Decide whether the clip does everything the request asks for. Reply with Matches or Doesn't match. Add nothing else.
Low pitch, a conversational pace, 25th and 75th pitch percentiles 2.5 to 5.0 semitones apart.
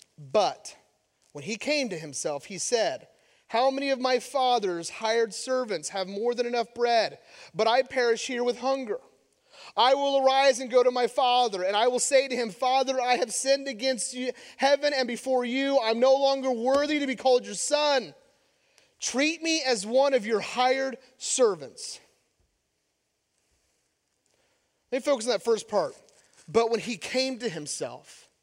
Doesn't match